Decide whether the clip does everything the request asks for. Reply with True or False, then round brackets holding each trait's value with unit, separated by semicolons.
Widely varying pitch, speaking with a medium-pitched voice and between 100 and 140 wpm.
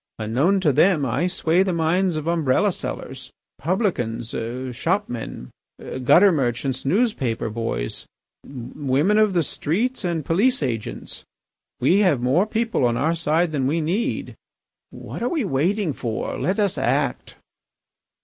True (6.8 semitones; 160 Hz; 135 wpm)